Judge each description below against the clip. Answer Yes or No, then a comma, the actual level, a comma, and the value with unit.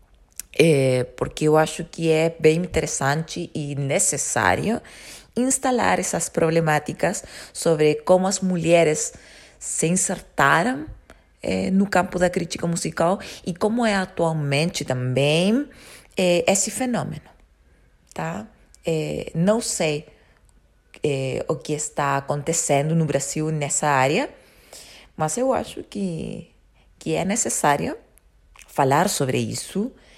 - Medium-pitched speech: Yes, medium, 165 Hz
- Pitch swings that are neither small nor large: Yes, average, 4.1 semitones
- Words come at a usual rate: No, slow, 110 wpm